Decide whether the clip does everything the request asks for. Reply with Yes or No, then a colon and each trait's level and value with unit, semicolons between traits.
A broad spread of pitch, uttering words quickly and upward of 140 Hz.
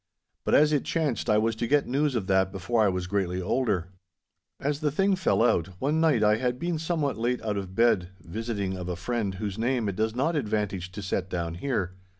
No: wide, 6.0 semitones; fast, 220 wpm; low, 110 Hz